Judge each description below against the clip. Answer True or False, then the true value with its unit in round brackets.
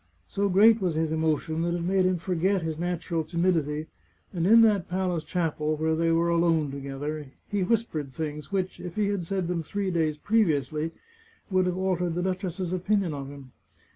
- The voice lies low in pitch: False (170 Hz)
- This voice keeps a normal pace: True (190 wpm)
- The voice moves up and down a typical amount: True (3.1 semitones)